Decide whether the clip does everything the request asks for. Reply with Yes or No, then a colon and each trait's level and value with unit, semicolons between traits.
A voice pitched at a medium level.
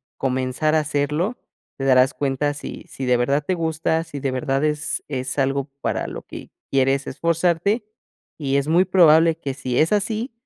Yes: medium, 145 Hz